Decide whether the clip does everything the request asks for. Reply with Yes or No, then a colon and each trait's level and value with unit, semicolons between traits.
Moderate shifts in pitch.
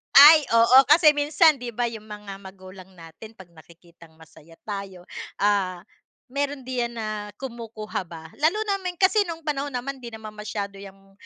No: wide, 6.3 semitones